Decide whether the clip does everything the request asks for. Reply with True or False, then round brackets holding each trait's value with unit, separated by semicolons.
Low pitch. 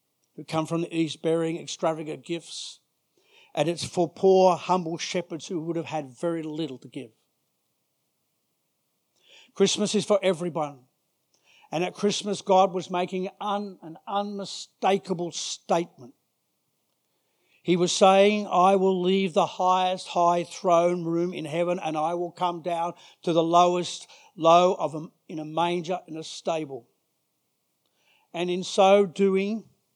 False (175 Hz)